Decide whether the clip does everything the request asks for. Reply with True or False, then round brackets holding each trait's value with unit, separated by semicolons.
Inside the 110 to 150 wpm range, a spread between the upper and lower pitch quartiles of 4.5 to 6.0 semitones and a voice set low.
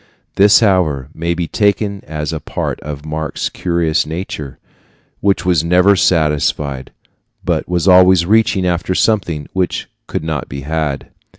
False (140 wpm; 3.4 semitones; 85 Hz)